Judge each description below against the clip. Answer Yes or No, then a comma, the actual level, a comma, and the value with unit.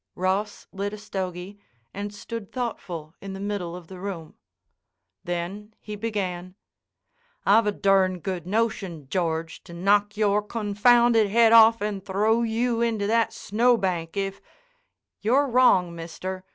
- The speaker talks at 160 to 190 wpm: No, average, 140 wpm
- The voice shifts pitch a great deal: No, average, 3.3 semitones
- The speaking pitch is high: Yes, high, 200 Hz